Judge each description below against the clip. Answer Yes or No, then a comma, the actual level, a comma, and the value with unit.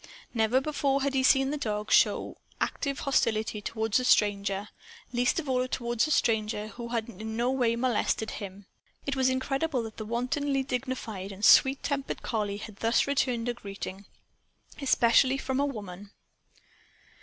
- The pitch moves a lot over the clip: No, average, 3.8 semitones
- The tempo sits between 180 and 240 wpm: No, average, 160 wpm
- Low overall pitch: No, high, 240 Hz